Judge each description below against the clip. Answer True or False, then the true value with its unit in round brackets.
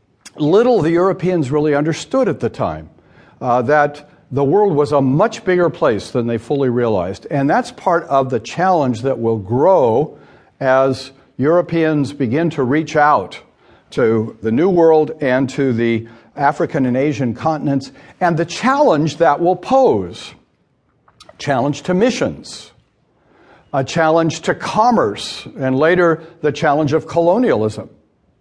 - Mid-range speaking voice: True (150 Hz)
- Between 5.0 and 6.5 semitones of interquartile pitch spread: False (4.2 semitones)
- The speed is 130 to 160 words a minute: True (140 wpm)